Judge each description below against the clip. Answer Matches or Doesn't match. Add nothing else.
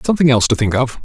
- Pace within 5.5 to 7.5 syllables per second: Doesn't match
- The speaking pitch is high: Doesn't match